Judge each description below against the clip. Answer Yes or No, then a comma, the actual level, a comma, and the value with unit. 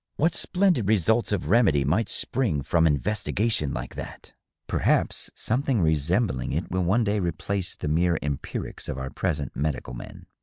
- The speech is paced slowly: No, average, 160 wpm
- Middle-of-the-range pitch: No, very low, 90 Hz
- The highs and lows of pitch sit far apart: Yes, wide, 6.8 semitones